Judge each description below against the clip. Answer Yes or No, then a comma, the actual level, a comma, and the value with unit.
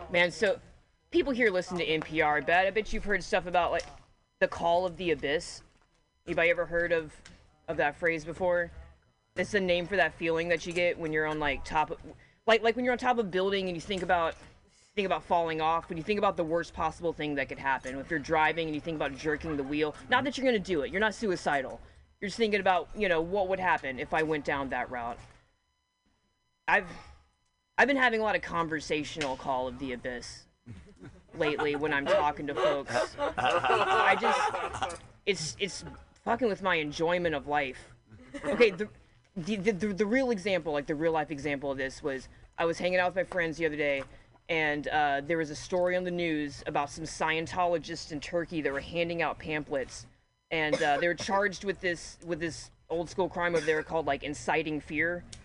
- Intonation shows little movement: No, average, 3.5 semitones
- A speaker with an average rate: No, fast, 210 wpm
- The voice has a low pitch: No, medium, 165 Hz